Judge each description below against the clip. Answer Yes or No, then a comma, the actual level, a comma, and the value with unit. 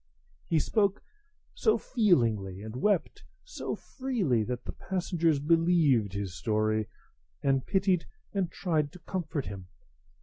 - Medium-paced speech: No, slow, 125 wpm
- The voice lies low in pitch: No, medium, 155 Hz